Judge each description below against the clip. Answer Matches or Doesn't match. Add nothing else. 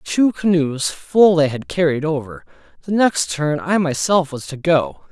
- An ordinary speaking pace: Matches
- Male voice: Matches